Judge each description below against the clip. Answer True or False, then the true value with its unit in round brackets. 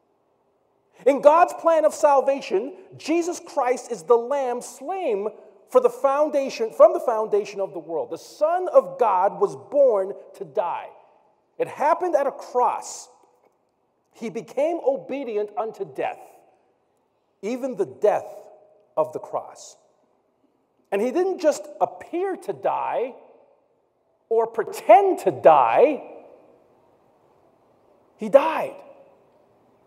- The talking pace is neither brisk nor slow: False (115 wpm)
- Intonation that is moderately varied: False (7.3 semitones)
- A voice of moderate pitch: False (275 Hz)